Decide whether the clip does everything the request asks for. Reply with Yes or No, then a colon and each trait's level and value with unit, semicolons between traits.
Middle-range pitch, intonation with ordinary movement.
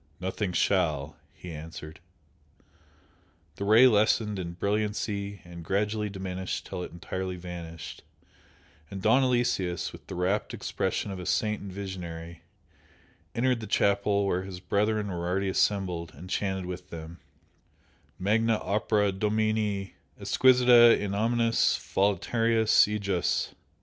No: low, 100 Hz; average, 3.0 semitones